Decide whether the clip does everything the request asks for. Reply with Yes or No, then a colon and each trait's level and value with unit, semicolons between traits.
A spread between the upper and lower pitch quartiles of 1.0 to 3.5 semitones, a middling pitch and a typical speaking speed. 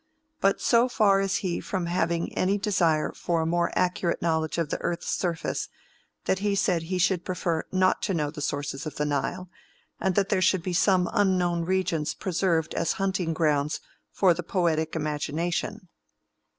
Yes: average, 2.8 semitones; medium, 175 Hz; average, 175 wpm